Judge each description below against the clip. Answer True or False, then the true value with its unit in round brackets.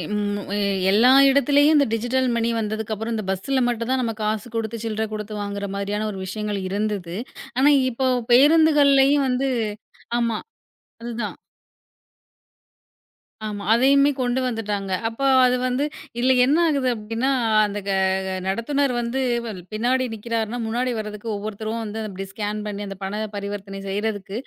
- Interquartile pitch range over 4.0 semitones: False (3.7 semitones)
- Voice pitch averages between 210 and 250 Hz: True (225 Hz)